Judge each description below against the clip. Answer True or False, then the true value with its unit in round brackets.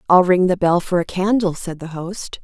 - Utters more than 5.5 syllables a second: False (4.9 syllables/s)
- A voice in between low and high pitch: True (180 Hz)